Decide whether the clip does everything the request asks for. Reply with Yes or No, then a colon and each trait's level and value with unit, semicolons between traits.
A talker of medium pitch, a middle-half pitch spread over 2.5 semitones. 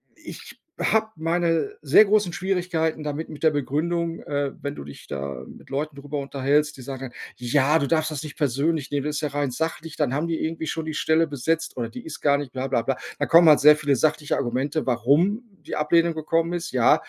Yes: medium, 150 Hz; average, 2.9 semitones